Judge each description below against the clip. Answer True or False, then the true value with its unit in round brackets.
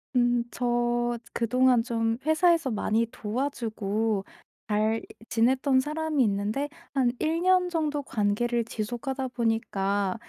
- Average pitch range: True (3.5 semitones)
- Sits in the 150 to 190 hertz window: False (240 Hz)